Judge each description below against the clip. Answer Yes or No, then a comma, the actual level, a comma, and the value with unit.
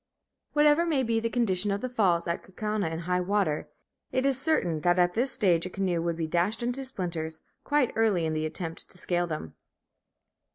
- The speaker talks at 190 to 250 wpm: Yes, average, 200 wpm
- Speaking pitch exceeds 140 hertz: Yes, medium, 185 Hz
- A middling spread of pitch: No, wide, 5.9 semitones